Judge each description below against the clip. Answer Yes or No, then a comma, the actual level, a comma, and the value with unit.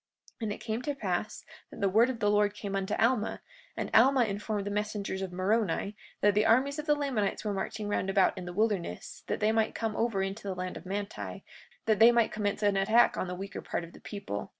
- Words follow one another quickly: Yes, fast, 240 wpm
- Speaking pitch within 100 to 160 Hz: No, high, 205 Hz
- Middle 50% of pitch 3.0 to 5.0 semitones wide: No, narrow, 2.5 semitones